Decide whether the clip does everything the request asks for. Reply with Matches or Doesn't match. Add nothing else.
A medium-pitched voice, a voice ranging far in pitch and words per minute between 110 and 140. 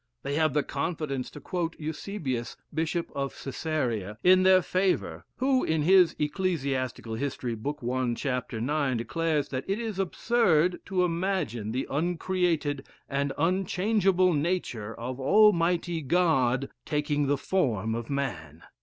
Matches